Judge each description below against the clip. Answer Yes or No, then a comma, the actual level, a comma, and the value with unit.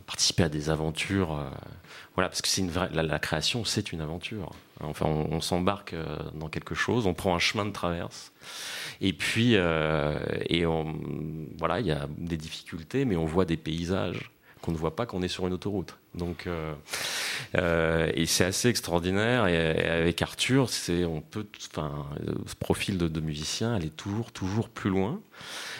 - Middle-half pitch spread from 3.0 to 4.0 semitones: Yes, average, 3.6 semitones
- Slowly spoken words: No, average, 185 wpm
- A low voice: Yes, very low, 85 Hz